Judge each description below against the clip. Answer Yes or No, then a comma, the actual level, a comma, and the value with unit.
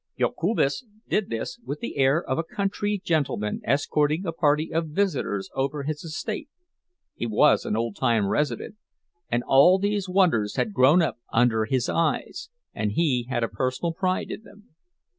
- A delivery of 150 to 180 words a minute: Yes, average, 165 wpm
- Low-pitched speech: No, medium, 150 Hz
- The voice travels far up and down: Yes, wide, 6.9 semitones